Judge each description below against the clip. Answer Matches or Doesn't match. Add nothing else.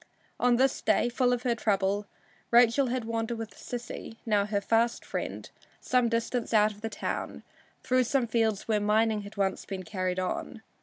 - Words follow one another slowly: Doesn't match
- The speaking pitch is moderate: Doesn't match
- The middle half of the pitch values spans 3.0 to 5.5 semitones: Doesn't match